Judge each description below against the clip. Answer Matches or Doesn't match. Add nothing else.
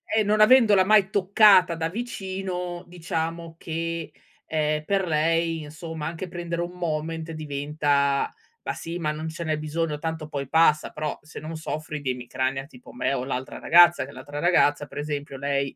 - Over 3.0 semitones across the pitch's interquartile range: Doesn't match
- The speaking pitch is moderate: Matches